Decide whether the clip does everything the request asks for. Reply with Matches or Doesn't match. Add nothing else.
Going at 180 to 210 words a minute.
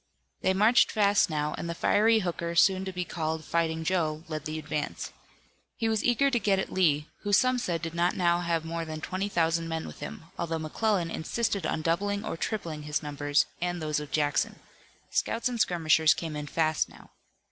Matches